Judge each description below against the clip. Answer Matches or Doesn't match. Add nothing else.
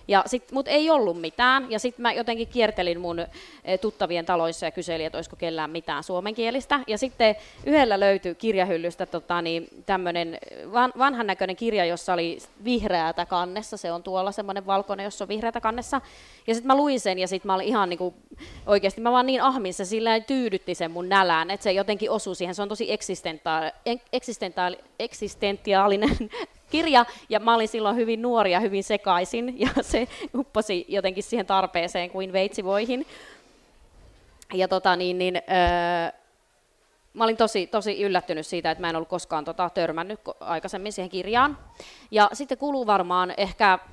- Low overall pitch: Doesn't match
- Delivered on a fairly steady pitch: Doesn't match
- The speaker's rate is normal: Doesn't match